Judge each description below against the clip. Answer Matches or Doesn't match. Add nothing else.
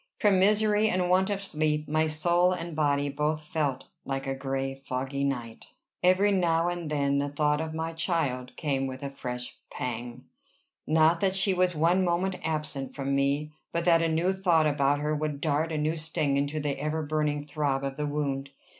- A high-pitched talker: Doesn't match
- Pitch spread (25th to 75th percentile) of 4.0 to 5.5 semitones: Doesn't match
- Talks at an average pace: Matches